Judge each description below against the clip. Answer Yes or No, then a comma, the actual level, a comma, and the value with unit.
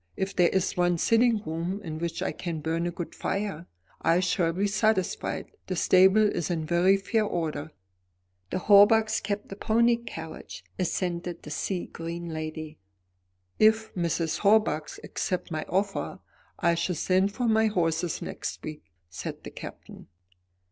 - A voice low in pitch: No, medium, 180 Hz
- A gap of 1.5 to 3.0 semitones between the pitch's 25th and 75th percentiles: No, average, 3.6 semitones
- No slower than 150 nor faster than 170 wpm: Yes, average, 155 wpm